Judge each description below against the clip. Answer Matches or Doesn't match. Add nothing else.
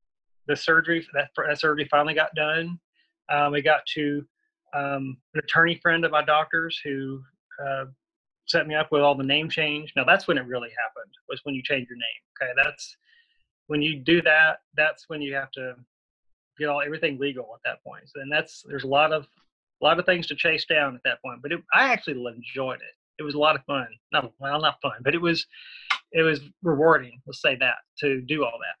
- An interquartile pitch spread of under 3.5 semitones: Matches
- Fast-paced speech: Matches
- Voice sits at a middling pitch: Matches